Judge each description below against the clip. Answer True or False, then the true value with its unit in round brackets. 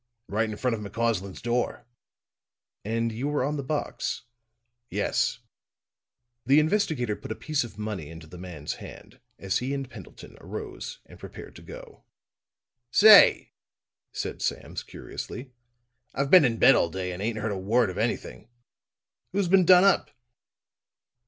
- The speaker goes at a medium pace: True (150 wpm)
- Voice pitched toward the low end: True (115 Hz)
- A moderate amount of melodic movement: False (5.9 semitones)